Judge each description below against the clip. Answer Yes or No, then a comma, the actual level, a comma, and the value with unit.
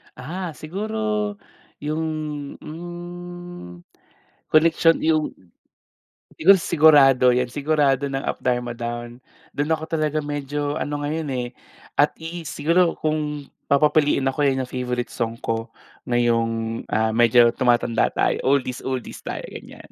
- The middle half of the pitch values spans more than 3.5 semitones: Yes, average, 4.5 semitones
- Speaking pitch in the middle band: Yes, medium, 145 Hz